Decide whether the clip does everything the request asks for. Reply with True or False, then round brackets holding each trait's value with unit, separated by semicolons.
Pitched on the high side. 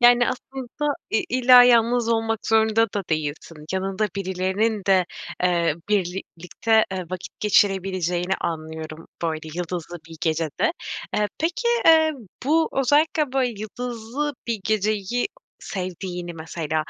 True (205 Hz)